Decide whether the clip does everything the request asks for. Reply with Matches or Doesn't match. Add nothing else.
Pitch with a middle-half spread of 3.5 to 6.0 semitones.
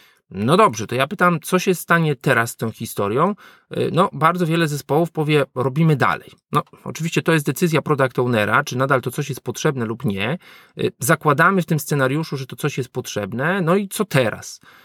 Matches